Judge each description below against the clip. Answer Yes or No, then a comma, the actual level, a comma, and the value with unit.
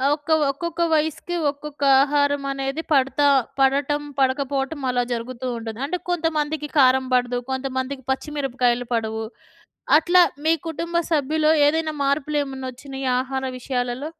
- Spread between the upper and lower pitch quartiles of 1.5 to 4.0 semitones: Yes, narrow, 2.6 semitones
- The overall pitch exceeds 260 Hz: Yes, very high, 275 Hz